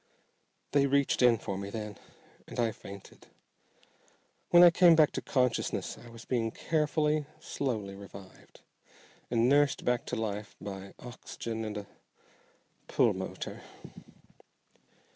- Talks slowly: Yes, slow, 125 wpm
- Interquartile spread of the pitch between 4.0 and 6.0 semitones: Yes, average, 5.2 semitones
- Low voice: Yes, low, 115 Hz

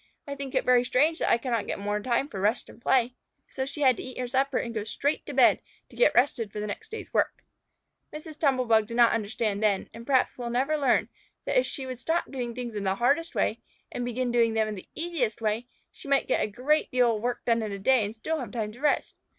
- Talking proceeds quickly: Yes, fast, 260 wpm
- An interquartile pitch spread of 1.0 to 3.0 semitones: No, average, 3.7 semitones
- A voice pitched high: Yes, high, 245 Hz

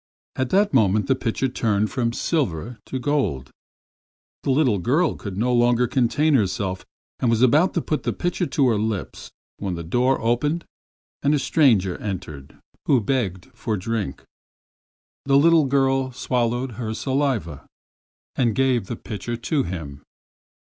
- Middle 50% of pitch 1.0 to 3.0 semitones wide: No, average, 4.8 semitones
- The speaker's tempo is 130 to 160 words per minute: Yes, average, 155 wpm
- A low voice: Yes, low, 120 Hz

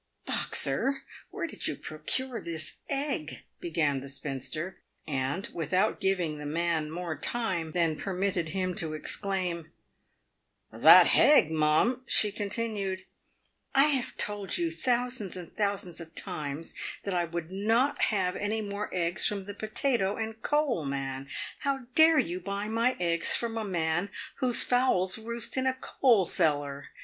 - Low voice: No, high, 190 Hz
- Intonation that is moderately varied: No, wide, 5.9 semitones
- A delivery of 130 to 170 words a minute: Yes, average, 160 wpm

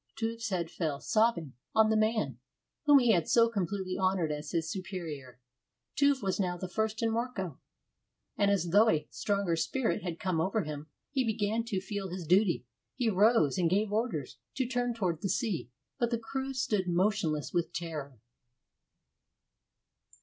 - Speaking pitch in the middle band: No, high, 195 Hz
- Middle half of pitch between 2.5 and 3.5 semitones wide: No, average, 5.0 semitones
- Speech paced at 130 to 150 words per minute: No, average, 165 wpm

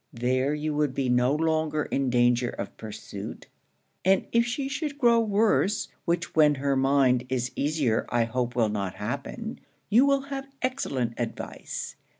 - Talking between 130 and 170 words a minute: Yes, average, 155 wpm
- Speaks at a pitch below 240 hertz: Yes, medium, 140 Hz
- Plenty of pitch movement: Yes, wide, 8.9 semitones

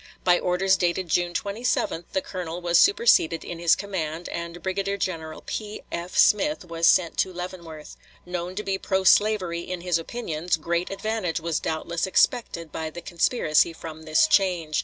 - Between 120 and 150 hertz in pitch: No, medium, 175 Hz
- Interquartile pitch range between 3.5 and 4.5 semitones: No, narrow, 2.4 semitones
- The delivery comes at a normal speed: Yes, average, 160 wpm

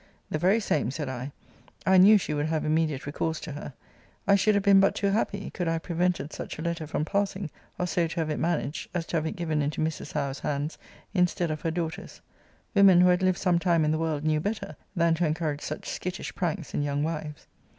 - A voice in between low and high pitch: Yes, medium, 165 Hz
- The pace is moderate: No, fast, 235 wpm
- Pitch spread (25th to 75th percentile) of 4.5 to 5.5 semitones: No, average, 2.9 semitones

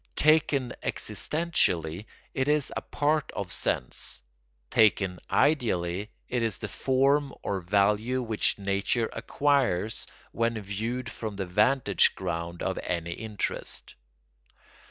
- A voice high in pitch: No, low, 110 Hz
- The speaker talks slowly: Yes, slow, 115 wpm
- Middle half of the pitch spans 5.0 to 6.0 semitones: Yes, wide, 5.4 semitones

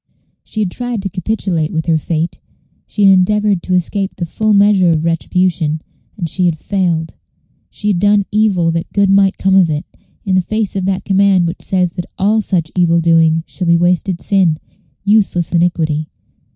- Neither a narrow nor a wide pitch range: Yes, average, 3.0 semitones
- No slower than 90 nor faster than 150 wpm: No, average, 185 wpm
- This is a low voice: No, medium, 185 Hz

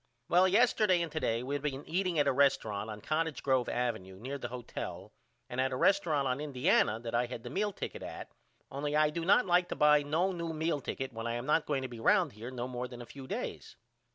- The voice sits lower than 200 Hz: Yes, medium, 140 Hz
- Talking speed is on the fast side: Yes, fast, 240 wpm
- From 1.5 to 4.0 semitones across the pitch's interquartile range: No, average, 4.9 semitones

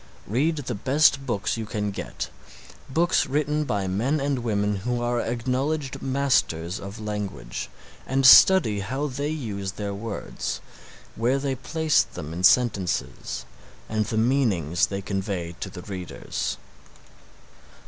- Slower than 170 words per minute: Yes, average, 140 wpm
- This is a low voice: Yes, low, 115 Hz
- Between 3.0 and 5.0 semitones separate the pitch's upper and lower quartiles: No, wide, 5.5 semitones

